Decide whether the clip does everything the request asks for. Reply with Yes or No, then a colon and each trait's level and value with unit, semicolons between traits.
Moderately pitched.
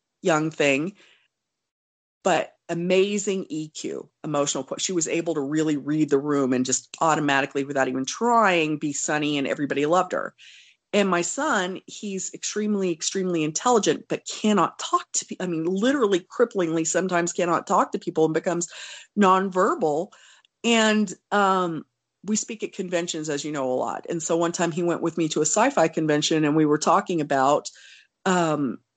Yes: medium, 170 Hz